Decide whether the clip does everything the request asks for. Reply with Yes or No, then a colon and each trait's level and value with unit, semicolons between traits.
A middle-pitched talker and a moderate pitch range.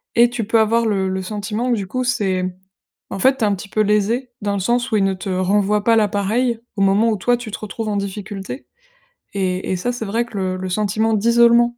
No: high, 210 Hz; average, 3.2 semitones